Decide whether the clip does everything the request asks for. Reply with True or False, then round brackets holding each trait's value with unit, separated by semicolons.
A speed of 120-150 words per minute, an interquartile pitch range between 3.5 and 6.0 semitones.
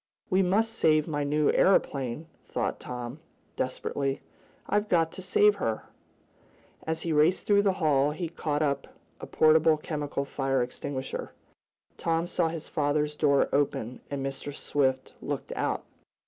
False (145 wpm; 3.0 semitones)